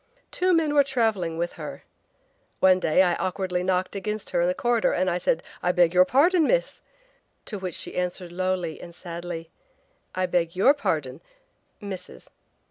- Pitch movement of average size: Yes, average, 3.6 semitones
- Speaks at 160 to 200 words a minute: Yes, average, 170 wpm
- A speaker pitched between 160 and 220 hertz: Yes, medium, 185 Hz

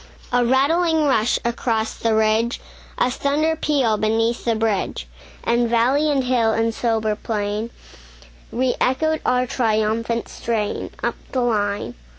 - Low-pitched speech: No, high, 235 Hz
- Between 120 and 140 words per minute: Yes, slow, 135 wpm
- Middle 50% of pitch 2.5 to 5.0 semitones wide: Yes, average, 2.8 semitones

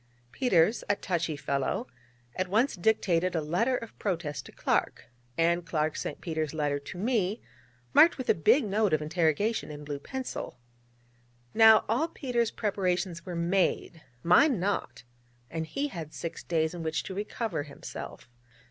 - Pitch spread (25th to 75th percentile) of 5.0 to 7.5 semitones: Yes, wide, 5.5 semitones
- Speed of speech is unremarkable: Yes, average, 155 wpm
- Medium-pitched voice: Yes, medium, 180 Hz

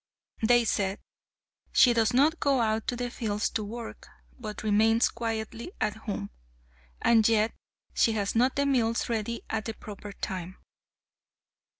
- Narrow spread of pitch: Yes, narrow, 2.1 semitones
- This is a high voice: Yes, high, 225 Hz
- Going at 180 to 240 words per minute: No, average, 150 wpm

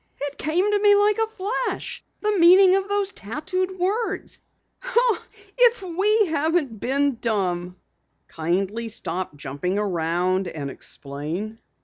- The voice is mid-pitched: No, very high, 310 Hz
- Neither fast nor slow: No, slow, 120 wpm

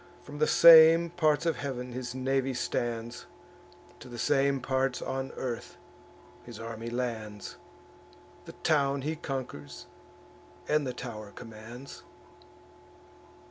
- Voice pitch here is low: Yes, low, 130 Hz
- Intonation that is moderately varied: Yes, average, 3.0 semitones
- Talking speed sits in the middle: No, slow, 115 wpm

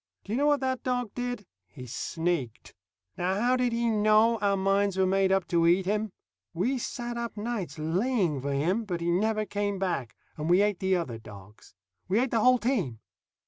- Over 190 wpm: Yes, average, 200 wpm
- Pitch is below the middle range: No, high, 200 Hz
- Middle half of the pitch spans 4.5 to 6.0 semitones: Yes, average, 5.2 semitones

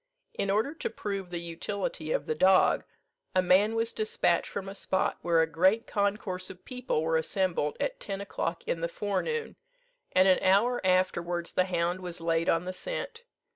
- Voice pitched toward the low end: No, medium, 185 Hz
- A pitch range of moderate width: Yes, average, 3.3 semitones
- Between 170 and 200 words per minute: Yes, average, 180 wpm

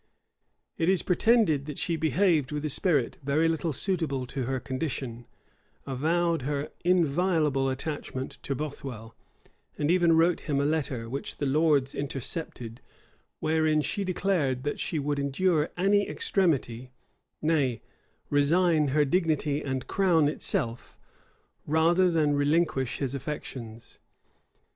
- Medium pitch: Yes, medium, 150 Hz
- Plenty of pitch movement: No, average, 3.6 semitones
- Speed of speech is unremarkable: No, slow, 125 wpm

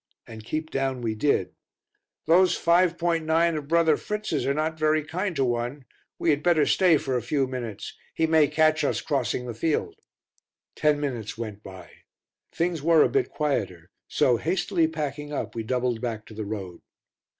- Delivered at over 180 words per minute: No, average, 170 wpm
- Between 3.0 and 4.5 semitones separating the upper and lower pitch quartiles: No, average, 5.3 semitones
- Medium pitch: Yes, medium, 145 Hz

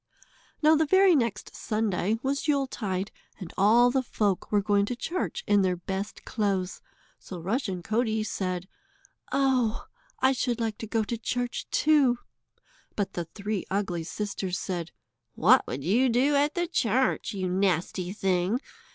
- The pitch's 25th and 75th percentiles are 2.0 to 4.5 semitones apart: No, average, 5.0 semitones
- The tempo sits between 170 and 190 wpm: No, average, 150 wpm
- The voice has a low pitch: No, high, 215 Hz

